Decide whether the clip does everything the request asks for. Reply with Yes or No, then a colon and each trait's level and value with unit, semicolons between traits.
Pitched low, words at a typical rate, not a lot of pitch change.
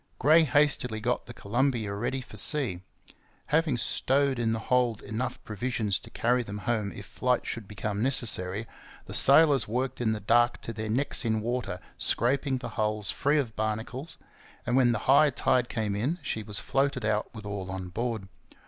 No: low, 120 Hz; average, 180 wpm; average, 3.5 semitones